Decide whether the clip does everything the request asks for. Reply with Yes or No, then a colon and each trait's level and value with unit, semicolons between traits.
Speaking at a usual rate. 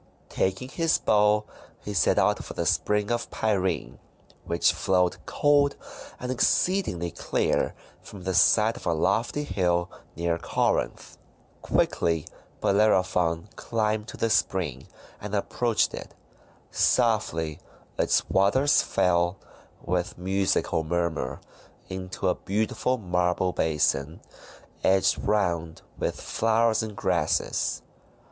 No: slow, 110 wpm